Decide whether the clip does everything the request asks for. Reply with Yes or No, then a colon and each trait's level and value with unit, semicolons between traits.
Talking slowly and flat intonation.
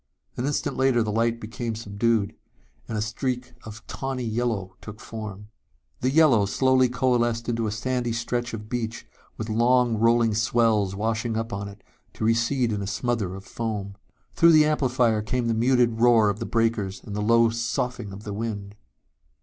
No: average, 175 wpm; narrow, 2.3 semitones